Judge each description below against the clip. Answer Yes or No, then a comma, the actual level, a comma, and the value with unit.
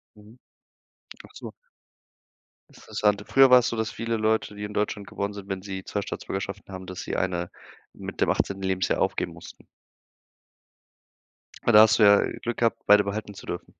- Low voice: Yes, low, 105 Hz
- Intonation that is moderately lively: No, narrow, 2.2 semitones